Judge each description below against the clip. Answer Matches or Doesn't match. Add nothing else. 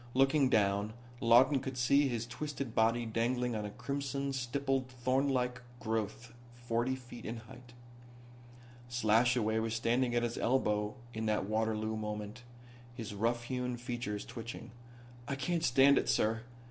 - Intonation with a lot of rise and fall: Doesn't match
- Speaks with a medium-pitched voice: Doesn't match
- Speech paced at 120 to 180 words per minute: Matches